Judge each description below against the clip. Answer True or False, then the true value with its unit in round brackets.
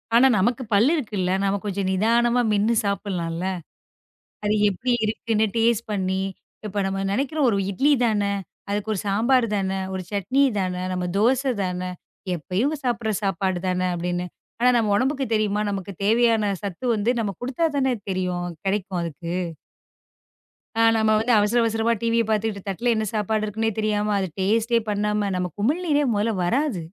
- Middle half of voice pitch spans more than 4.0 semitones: False (3.3 semitones)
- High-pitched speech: True (210 Hz)